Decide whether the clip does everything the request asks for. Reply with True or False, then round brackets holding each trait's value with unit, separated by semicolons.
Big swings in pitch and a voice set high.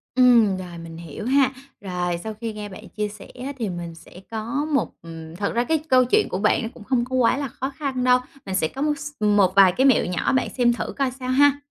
True (5.7 semitones; 225 Hz)